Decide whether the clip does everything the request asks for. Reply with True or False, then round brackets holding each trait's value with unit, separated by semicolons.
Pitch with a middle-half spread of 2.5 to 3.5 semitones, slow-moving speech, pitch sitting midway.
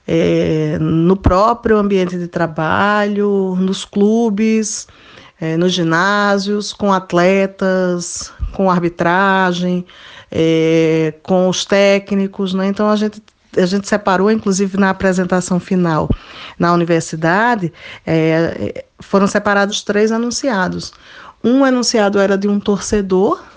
False (2.8 semitones; 110 wpm; 195 Hz)